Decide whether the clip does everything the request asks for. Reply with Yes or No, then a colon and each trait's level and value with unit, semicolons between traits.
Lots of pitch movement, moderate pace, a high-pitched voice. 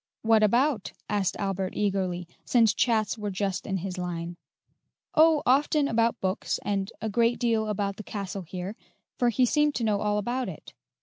No: average, 3.5 semitones; average, 175 wpm; high, 210 Hz